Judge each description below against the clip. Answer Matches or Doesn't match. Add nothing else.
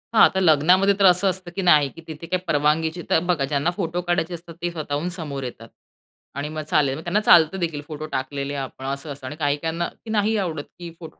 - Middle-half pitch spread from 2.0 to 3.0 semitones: Doesn't match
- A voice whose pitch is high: Doesn't match